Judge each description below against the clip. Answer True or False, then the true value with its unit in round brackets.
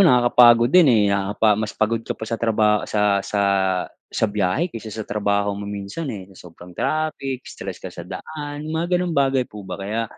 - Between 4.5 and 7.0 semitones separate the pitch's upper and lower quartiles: True (4.8 semitones)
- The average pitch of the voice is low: True (110 Hz)